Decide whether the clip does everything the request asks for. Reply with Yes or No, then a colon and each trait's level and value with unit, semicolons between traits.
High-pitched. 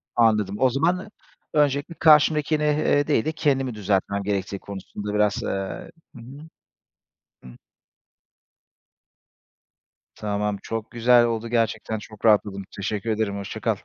No: low, 115 Hz